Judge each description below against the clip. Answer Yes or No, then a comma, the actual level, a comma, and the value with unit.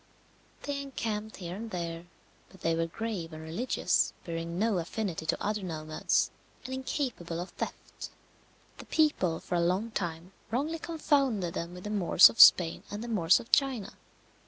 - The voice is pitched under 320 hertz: Yes, high, 190 Hz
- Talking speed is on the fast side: No, average, 165 wpm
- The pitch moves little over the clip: No, wide, 5.4 semitones